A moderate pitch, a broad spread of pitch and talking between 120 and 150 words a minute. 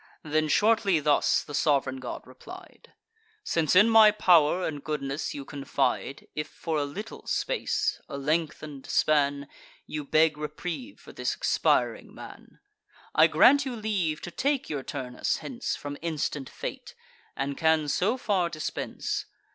Yes: medium, 155 Hz; wide, 6.1 semitones; average, 145 wpm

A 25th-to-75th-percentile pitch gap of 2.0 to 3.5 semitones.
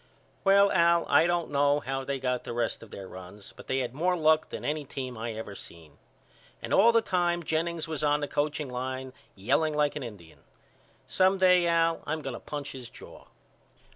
No: average, 5.1 semitones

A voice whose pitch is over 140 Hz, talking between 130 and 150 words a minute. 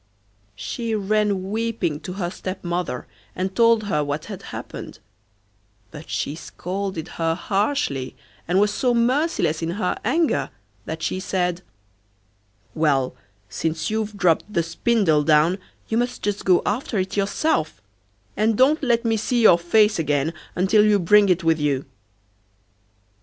Yes: high, 190 Hz; average, 140 wpm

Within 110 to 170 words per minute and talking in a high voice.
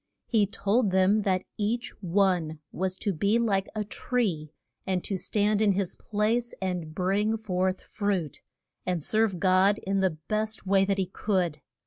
Yes: average, 160 wpm; high, 195 Hz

